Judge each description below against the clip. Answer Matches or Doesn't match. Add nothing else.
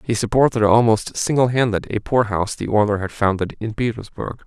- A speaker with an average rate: Matches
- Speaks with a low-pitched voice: Matches